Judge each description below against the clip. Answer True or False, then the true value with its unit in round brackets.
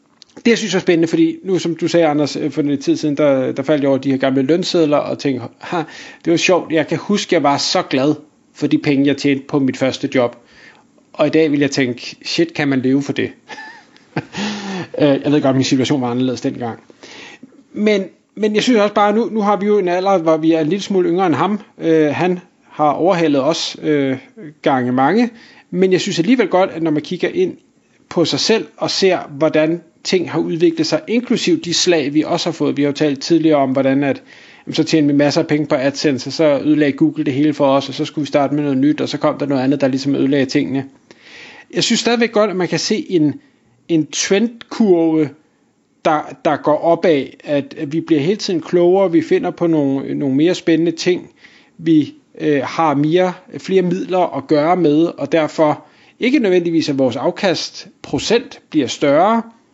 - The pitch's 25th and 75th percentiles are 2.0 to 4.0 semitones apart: False (4.5 semitones)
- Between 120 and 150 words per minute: False (215 wpm)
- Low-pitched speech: False (160 Hz)